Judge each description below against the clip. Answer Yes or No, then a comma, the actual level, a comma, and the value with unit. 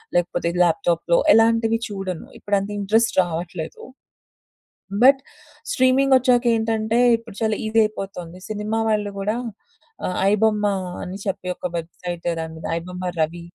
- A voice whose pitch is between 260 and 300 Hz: No, high, 200 Hz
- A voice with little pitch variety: No, average, 4.2 semitones